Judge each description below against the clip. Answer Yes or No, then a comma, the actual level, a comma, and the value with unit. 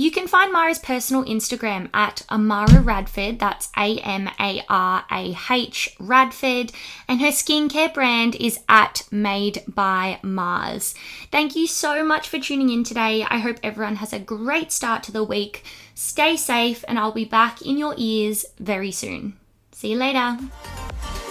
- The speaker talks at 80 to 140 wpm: No, average, 150 wpm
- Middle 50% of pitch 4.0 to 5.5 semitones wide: Yes, average, 4.5 semitones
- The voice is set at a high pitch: Yes, high, 230 Hz